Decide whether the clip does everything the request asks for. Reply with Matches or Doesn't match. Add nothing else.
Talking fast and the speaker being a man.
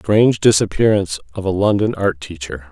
Doesn't match